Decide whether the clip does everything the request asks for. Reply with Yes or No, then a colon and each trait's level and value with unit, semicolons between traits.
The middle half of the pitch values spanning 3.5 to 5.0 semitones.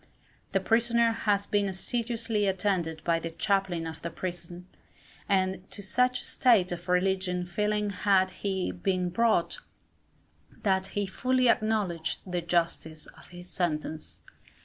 No: average, 3.0 semitones